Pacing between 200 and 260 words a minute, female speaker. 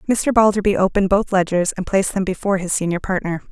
Yes: fast, 205 wpm; female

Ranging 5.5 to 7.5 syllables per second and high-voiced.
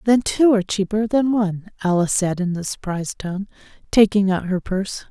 Yes: 5.7 syllables/s; high, 200 Hz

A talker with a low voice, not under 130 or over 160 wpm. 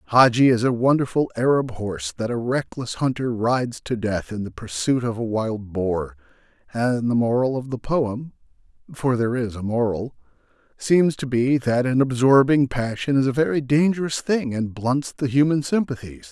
No: low, 125 Hz; average, 170 wpm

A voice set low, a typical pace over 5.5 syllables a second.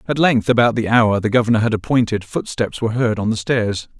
Yes: low, 115 Hz; 5.8 syllables/s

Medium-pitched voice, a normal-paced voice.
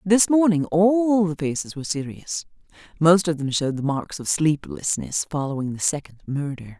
Yes: medium, 160 Hz; average, 170 wpm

